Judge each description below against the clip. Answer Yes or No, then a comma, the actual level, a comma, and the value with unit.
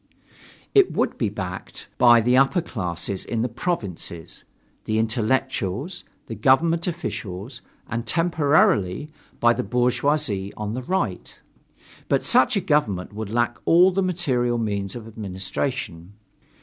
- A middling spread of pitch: No, wide, 6.6 semitones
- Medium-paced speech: No, slow, 130 wpm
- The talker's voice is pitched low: Yes, low, 120 Hz